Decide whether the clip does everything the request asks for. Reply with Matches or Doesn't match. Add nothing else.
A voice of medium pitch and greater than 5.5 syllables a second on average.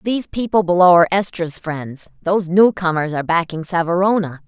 Matches